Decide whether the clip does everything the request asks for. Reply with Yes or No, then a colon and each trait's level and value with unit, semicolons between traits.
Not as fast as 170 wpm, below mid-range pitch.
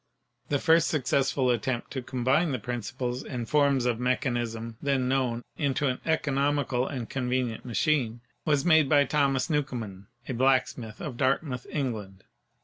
Yes: average, 140 wpm; low, 130 Hz